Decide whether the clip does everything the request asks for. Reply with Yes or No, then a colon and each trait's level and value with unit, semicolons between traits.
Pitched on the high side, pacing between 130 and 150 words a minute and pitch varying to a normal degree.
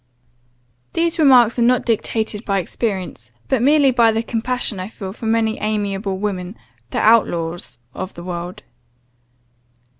Yes: high, 220 Hz; average, 140 wpm; average, 3.8 semitones